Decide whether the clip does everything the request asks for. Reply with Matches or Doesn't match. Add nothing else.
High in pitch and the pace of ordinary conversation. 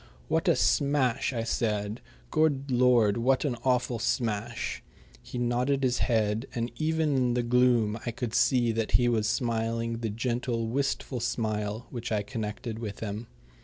Doesn't match